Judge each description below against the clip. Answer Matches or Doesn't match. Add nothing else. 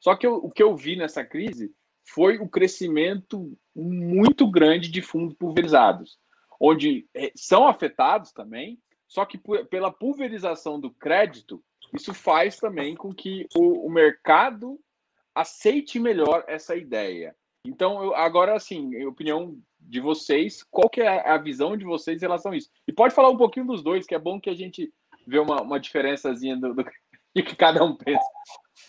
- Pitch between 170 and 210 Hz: Matches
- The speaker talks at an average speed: Matches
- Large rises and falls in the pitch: Matches